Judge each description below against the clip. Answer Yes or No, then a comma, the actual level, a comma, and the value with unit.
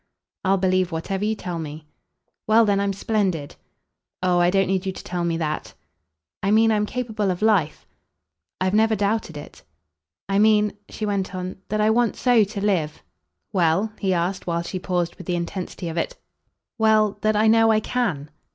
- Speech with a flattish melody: No, average, 3.4 semitones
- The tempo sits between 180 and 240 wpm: Yes, average, 190 wpm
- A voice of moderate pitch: No, high, 195 Hz